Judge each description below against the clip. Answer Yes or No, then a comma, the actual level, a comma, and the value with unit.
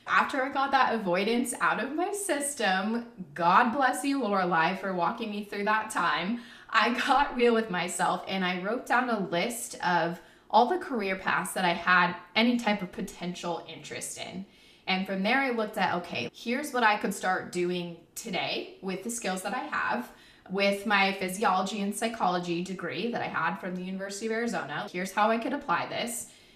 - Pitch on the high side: Yes, high, 200 Hz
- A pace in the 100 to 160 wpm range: No, average, 190 wpm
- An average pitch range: Yes, average, 4.5 semitones